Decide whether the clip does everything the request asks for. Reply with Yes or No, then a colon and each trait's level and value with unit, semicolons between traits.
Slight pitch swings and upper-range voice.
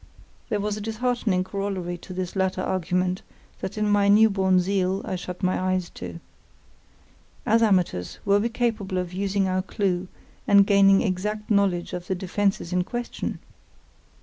Yes: narrow, 2.0 semitones; high, 195 Hz